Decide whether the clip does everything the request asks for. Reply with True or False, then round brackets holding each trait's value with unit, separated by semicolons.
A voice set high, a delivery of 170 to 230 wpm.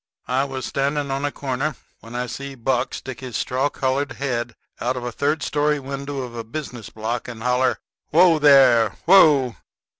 False (135 Hz; 180 wpm)